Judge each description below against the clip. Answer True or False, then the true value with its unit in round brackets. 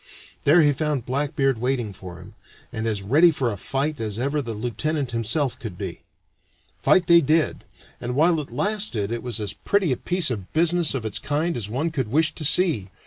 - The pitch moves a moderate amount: False (5.7 semitones)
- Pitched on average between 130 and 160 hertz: True (135 Hz)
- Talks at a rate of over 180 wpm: True (200 wpm)